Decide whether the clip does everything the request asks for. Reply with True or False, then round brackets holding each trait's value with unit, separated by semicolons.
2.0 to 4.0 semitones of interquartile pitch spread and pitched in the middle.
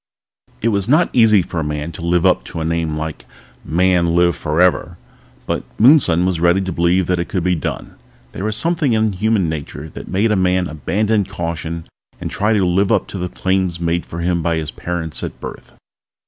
False (3.1 semitones; 90 Hz)